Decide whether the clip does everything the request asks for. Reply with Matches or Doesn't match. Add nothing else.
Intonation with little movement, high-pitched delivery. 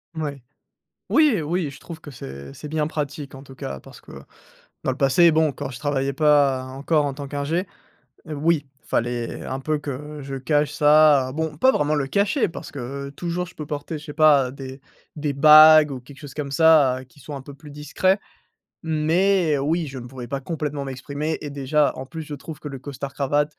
Doesn't match